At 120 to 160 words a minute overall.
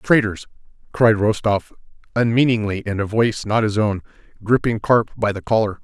Yes: average, 155 wpm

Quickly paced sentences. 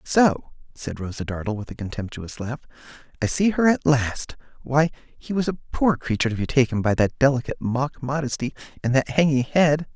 No: average, 185 wpm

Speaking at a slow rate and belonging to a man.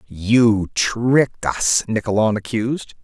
Yes: slow, 100 wpm; male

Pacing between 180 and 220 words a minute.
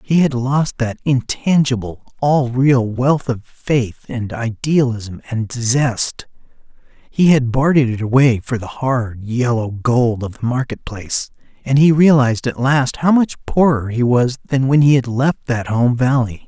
No: average, 165 wpm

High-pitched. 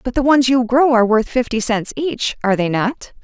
Yes: high, 240 Hz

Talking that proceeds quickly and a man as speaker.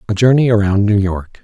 Yes: fast, 210 wpm; male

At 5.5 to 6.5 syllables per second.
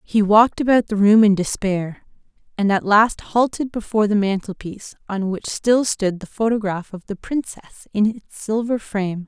No: 5.1 syllables/s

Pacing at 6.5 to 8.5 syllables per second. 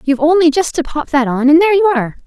Yes: 7.1 syllables/s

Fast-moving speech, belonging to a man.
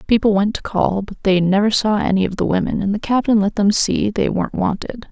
No: fast, 245 wpm; female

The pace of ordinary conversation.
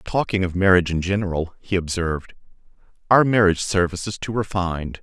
Yes: average, 155 wpm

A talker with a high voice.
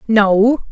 Yes: high, 220 Hz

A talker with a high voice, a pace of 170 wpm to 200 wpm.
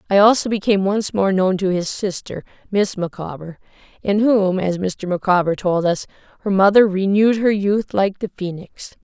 Yes: high, 195 Hz; average, 175 wpm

